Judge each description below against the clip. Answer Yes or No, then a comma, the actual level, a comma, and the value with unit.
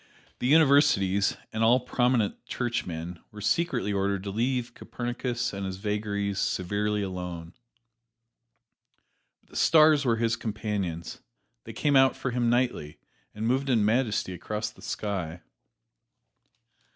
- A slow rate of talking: Yes, slow, 125 wpm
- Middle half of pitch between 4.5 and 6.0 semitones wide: No, average, 3.9 semitones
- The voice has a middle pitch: No, low, 105 Hz